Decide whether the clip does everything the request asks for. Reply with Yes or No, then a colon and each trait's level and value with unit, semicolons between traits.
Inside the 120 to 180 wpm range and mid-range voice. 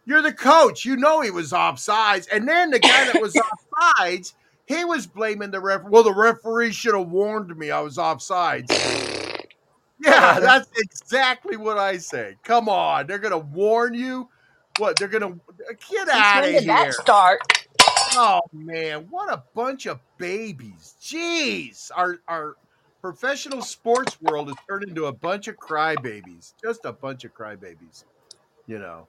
No: average, 165 wpm; high, 205 Hz